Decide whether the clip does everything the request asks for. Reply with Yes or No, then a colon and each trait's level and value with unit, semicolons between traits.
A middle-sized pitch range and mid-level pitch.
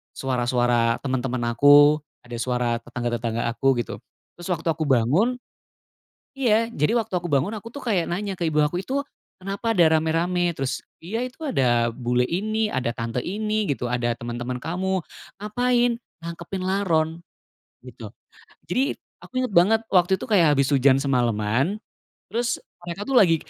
No: wide, 8.3 semitones; medium, 160 Hz